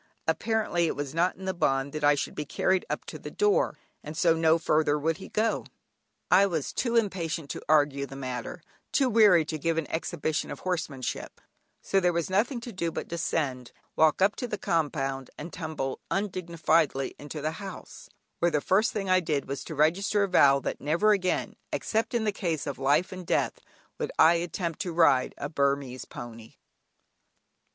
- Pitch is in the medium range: Yes, medium, 165 Hz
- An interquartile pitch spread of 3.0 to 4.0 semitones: No, average, 4.4 semitones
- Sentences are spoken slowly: No, average, 190 wpm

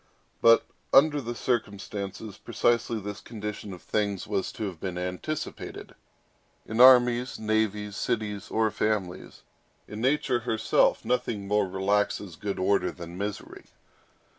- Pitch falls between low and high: No, low, 105 Hz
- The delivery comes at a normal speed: No, slow, 125 wpm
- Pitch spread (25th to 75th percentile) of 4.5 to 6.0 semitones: No, average, 2.9 semitones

